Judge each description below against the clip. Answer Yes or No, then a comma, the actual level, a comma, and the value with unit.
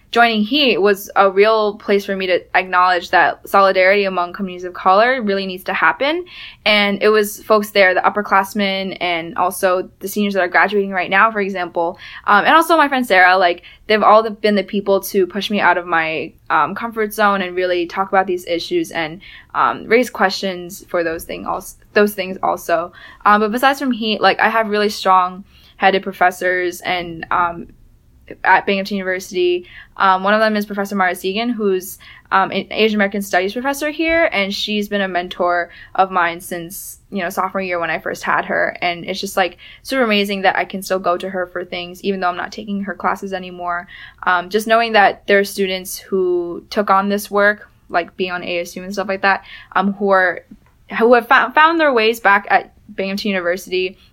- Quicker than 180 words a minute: Yes, average, 200 wpm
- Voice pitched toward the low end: No, high, 195 Hz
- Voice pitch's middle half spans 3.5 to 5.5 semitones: No, narrow, 2.5 semitones